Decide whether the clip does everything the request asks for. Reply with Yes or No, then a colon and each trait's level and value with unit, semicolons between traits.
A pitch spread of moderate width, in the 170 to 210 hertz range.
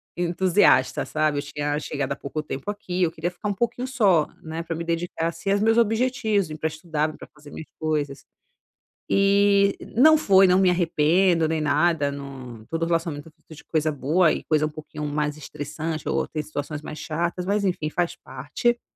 No: average, 3.9 semitones; medium, 160 Hz